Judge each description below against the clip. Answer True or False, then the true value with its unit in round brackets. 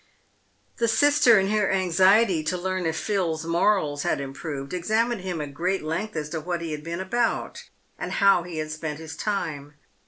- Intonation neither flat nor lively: True (4.2 semitones)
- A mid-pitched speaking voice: True (175 Hz)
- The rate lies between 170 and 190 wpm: True (185 wpm)